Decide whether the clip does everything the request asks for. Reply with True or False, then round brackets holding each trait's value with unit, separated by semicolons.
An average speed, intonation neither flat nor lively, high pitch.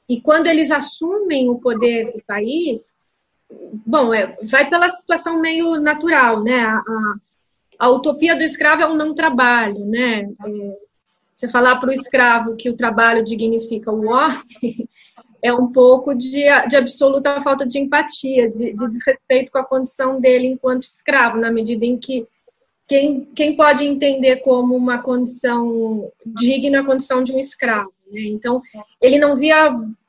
True (155 wpm; 3.5 semitones; 255 Hz)